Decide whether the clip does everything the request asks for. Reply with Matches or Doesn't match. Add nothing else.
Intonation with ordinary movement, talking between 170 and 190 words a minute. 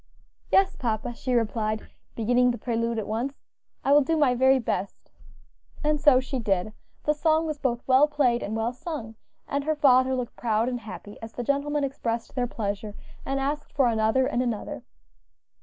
Matches